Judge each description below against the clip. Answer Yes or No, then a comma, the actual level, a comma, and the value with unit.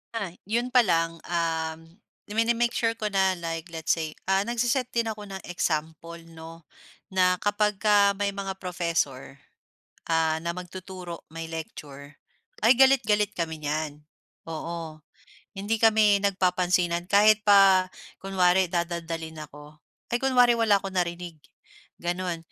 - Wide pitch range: No, average, 3.9 semitones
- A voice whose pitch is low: No, medium, 180 Hz